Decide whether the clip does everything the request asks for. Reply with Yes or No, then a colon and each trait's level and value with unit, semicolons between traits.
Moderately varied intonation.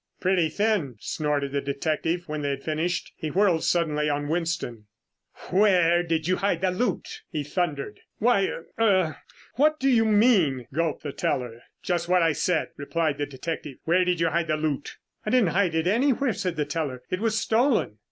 Yes: average, 4.5 semitones